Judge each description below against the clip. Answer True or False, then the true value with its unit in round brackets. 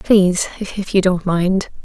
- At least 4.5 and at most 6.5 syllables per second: False (4.0 syllables/s)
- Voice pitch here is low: False (185 Hz)